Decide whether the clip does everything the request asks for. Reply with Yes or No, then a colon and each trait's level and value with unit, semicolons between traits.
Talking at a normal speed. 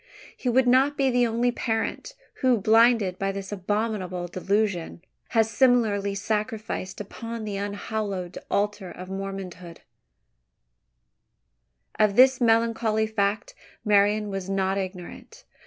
No: slow, 115 wpm